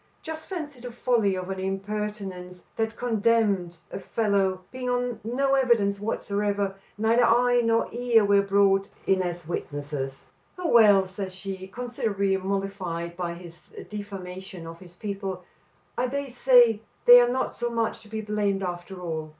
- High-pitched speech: Yes, high, 200 Hz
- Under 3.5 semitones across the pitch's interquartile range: No, average, 3.8 semitones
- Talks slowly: No, average, 155 wpm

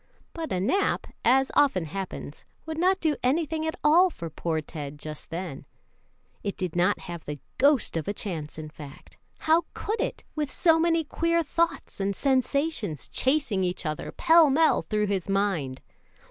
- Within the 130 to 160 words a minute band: No, average, 170 wpm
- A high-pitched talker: Yes, high, 215 Hz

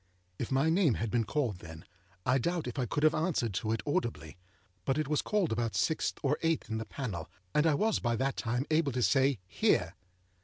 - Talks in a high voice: No, low, 130 Hz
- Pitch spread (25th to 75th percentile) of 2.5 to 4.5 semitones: No, average, 5.2 semitones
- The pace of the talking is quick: Yes, fast, 220 wpm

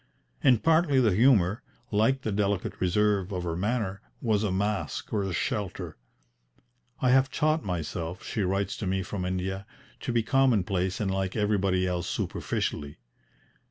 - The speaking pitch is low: Yes, low, 100 Hz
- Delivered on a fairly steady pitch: No, average, 3.5 semitones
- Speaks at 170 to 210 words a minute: No, average, 155 wpm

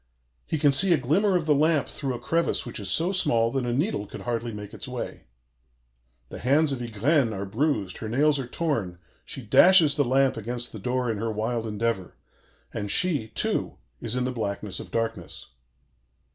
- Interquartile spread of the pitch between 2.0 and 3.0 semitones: No, average, 5.1 semitones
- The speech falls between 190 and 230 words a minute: Yes, average, 195 wpm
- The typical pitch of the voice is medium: No, low, 125 Hz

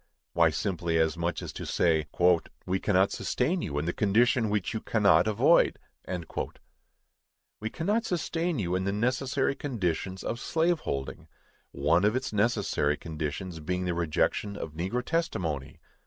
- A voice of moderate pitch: No, very low, 95 Hz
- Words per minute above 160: No, average, 150 wpm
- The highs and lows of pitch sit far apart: Yes, wide, 6.6 semitones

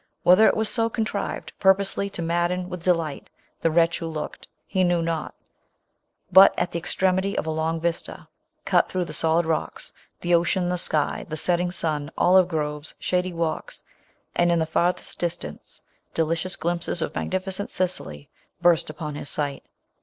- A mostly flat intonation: Yes, narrow, 2.3 semitones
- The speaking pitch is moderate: Yes, medium, 170 Hz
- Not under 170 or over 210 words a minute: Yes, average, 175 wpm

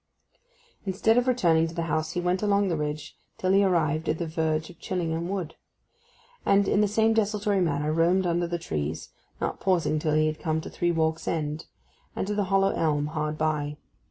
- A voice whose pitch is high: No, medium, 165 Hz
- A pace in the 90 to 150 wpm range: No, average, 195 wpm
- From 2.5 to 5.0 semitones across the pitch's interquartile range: Yes, average, 3.7 semitones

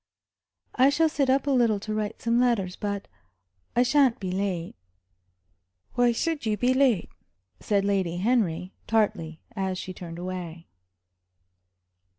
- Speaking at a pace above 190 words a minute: No, average, 140 wpm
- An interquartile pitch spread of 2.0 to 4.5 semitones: No, average, 5.0 semitones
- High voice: Yes, high, 210 Hz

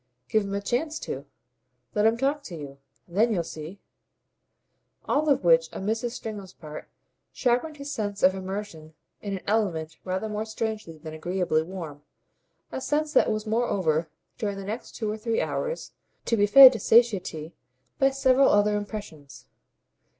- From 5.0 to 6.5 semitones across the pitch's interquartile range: Yes, wide, 5.4 semitones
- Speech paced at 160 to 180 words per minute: Yes, average, 165 wpm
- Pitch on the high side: Yes, high, 205 Hz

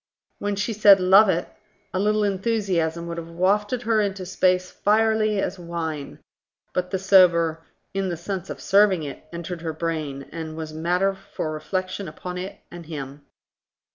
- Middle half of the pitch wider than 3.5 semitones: No, average, 3.2 semitones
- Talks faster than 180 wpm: No, average, 165 wpm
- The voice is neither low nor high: Yes, medium, 180 Hz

